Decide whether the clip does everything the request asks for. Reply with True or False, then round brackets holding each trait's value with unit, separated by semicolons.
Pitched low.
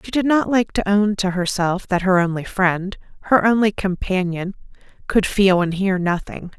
False (195 Hz)